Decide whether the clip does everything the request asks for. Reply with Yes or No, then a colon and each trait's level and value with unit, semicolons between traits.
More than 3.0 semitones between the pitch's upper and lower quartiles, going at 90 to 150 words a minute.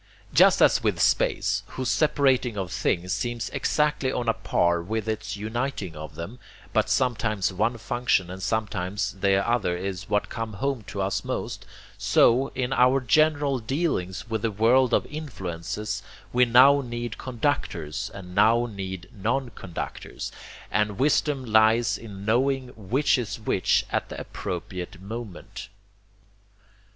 Yes: average, 4.5 semitones; average, 140 wpm